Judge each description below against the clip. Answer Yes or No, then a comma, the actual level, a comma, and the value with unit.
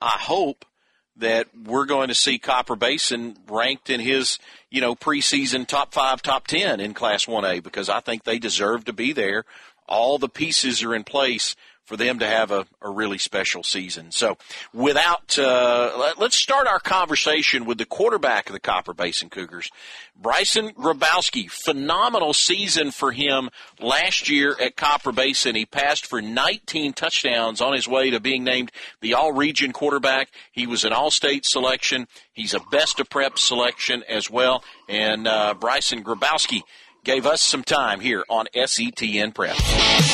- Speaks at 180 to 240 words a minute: No, average, 170 wpm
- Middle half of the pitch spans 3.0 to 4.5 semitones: Yes, average, 3.8 semitones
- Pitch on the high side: No, low, 130 Hz